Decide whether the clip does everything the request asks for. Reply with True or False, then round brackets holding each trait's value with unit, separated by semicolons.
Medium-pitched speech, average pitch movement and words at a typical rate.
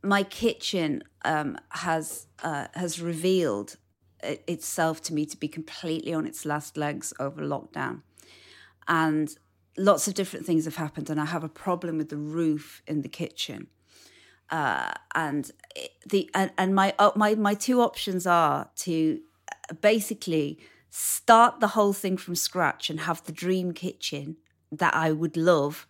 True (170 Hz; 3.7 semitones; 160 wpm)